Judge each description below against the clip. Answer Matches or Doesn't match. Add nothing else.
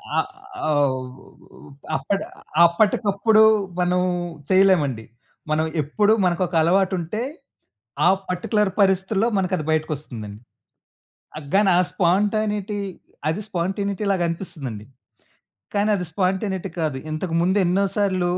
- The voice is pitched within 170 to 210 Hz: Matches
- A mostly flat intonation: Doesn't match